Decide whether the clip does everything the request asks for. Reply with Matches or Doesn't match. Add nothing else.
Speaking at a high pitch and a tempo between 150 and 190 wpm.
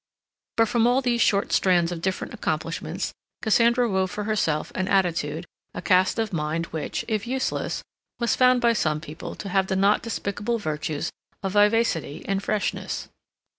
Matches